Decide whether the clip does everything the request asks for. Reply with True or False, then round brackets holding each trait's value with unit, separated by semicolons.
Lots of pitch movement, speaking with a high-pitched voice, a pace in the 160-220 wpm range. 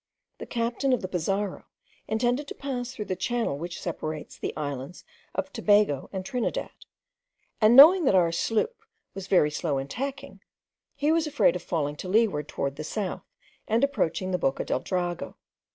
True (6.7 semitones; 195 Hz; 170 wpm)